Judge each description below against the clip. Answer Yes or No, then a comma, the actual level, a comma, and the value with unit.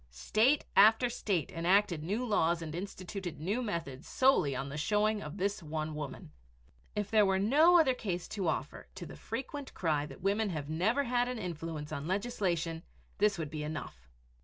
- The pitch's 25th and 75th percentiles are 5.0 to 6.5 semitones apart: Yes, wide, 5.6 semitones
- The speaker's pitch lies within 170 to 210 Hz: Yes, medium, 185 Hz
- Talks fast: No, average, 180 wpm